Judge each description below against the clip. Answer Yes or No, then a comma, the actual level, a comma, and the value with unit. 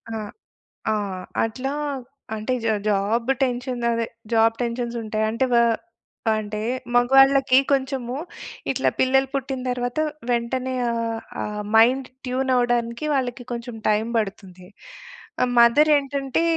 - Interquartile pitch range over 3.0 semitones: No, narrow, 2.6 semitones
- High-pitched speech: Yes, high, 245 Hz